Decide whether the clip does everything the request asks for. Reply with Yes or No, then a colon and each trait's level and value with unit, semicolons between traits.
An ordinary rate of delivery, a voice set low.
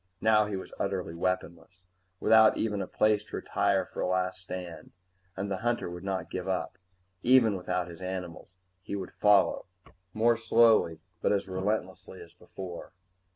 Yes: average, 160 wpm; very low, 95 Hz